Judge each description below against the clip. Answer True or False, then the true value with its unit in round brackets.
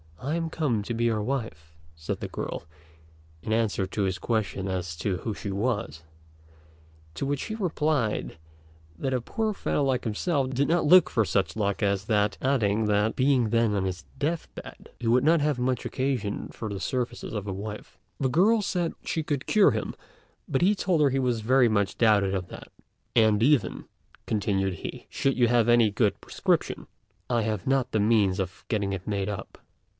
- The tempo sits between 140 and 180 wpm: False (190 wpm)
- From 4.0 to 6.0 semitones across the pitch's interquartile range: True (5.0 semitones)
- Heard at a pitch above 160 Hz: False (115 Hz)